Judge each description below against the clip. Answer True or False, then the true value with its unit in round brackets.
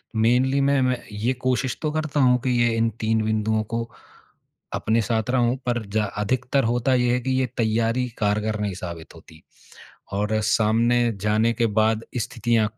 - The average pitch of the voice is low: True (115 Hz)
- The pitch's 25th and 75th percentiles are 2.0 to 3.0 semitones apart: True (2.5 semitones)